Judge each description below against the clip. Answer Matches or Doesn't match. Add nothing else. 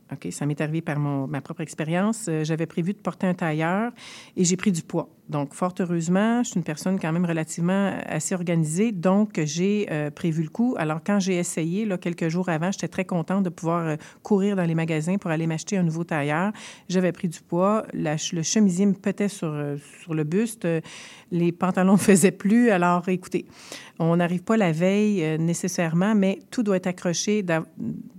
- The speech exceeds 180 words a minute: Matches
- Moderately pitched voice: Matches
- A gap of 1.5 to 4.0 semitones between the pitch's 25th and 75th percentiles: Matches